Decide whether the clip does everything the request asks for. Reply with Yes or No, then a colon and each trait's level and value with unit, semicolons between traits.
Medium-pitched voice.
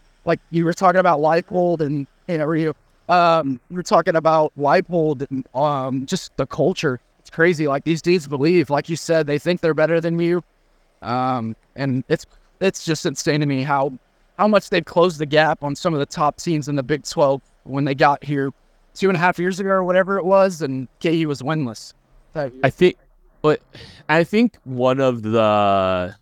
Yes: medium, 155 Hz